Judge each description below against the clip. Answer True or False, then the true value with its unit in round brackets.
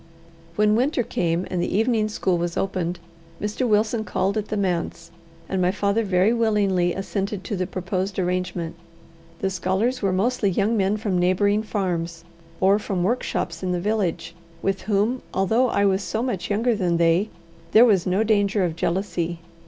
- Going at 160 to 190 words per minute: True (170 wpm)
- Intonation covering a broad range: False (3.0 semitones)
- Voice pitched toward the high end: True (195 Hz)